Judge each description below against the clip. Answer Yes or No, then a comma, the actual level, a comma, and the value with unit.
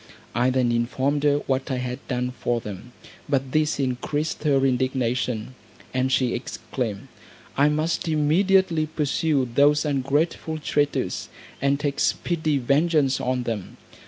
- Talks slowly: Yes, slow, 130 wpm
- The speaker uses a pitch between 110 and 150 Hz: Yes, low, 135 Hz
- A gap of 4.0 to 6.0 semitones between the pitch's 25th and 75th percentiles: No, average, 3.0 semitones